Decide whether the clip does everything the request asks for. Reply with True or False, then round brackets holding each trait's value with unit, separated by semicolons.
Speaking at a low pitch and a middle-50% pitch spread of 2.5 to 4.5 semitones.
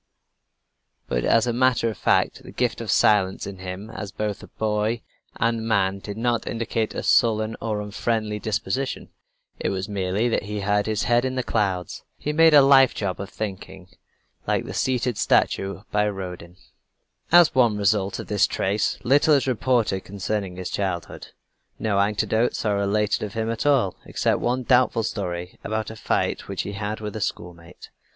True (105 Hz; 2.9 semitones)